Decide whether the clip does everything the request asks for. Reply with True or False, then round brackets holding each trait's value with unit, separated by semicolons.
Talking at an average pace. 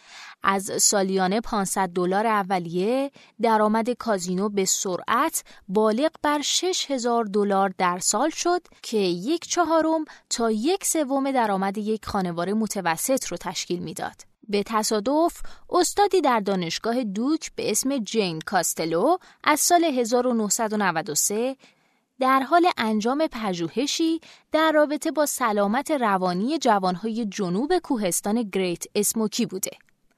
True (115 wpm)